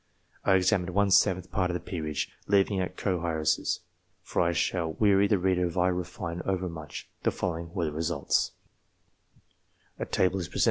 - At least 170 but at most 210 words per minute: No, average, 155 wpm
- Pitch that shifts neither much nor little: No, narrow, 2.1 semitones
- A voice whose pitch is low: Yes, very low, 90 Hz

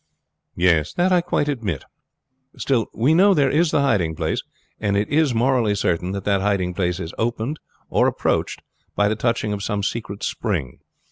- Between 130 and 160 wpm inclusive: No, average, 175 wpm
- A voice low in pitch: Yes, low, 105 Hz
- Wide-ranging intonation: Yes, wide, 6.2 semitones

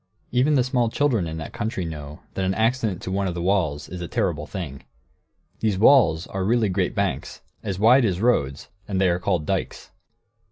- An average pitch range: Yes, average, 4.7 semitones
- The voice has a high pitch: No, very low, 95 Hz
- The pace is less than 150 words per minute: No, average, 200 wpm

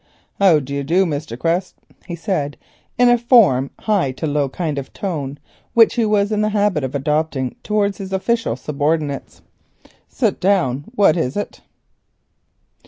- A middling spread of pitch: No, wide, 6.3 semitones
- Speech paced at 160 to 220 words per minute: No, average, 145 wpm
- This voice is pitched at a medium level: Yes, medium, 170 Hz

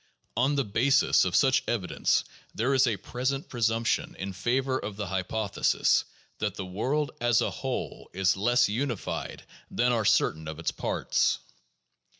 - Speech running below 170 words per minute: Yes, average, 150 wpm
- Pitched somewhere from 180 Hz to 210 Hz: No, low, 115 Hz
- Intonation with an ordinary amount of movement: Yes, average, 4.9 semitones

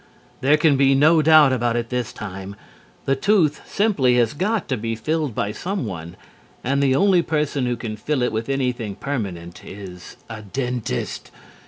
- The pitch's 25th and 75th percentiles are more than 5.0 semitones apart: Yes, wide, 5.5 semitones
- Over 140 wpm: Yes, average, 170 wpm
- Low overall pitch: Yes, low, 130 Hz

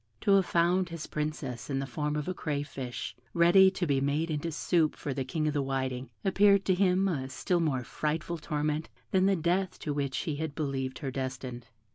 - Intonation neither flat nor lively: Yes, average, 4.2 semitones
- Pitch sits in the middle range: Yes, medium, 150 Hz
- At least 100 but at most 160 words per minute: No, fast, 205 wpm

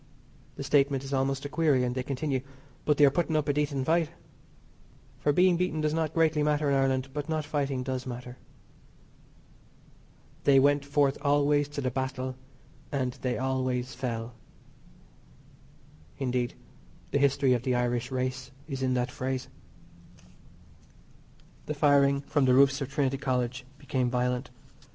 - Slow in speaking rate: No, average, 150 wpm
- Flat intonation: Yes, narrow, 2.2 semitones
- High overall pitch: No, low, 135 Hz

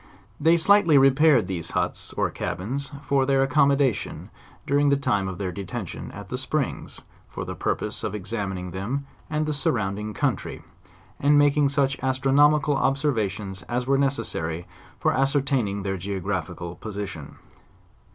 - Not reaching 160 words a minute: Yes, average, 150 wpm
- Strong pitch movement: Yes, wide, 6.3 semitones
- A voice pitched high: No, low, 130 Hz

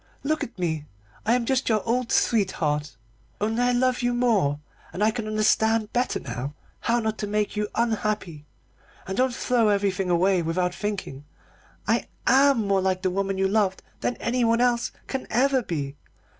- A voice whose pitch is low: No, high, 210 Hz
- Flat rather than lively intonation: No, average, 4.5 semitones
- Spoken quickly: No, average, 175 wpm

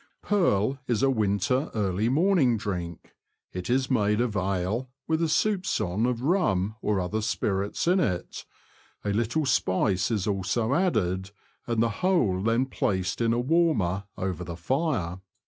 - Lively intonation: Yes, wide, 5.8 semitones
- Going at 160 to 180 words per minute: No, average, 150 wpm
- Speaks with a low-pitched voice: Yes, low, 110 Hz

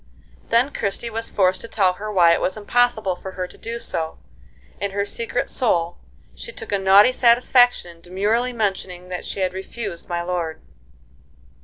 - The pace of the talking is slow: No, average, 180 wpm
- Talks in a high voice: Yes, high, 200 Hz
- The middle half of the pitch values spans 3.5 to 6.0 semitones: Yes, average, 4.2 semitones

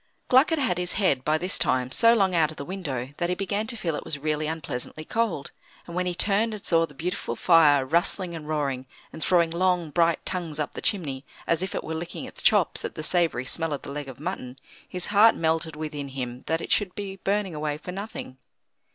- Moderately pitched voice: Yes, medium, 165 Hz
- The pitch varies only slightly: No, average, 4.0 semitones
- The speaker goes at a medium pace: No, fast, 230 wpm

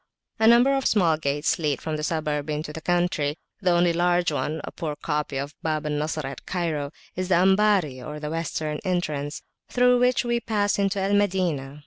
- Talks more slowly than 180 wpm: No, average, 195 wpm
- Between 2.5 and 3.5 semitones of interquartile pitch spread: No, average, 4.3 semitones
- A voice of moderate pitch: Yes, medium, 165 Hz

